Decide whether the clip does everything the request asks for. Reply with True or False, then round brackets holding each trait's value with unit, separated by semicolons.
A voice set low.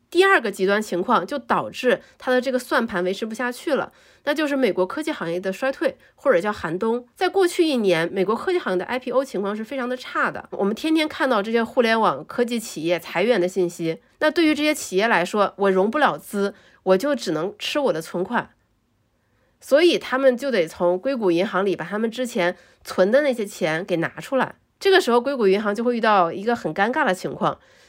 False (220 Hz)